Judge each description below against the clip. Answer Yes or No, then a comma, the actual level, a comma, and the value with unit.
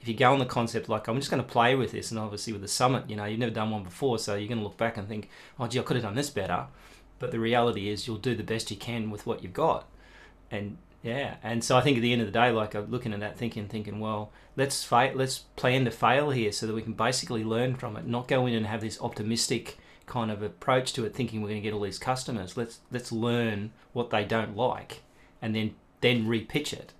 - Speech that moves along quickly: Yes, fast, 275 wpm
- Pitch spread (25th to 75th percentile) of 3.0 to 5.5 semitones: No, narrow, 2.6 semitones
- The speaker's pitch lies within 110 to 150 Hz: Yes, low, 115 Hz